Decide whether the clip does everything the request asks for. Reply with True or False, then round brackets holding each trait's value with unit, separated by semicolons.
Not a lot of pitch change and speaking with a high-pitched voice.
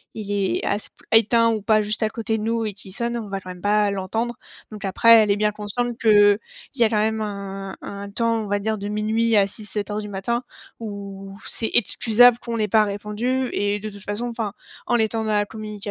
True (1.9 semitones; 210 Hz)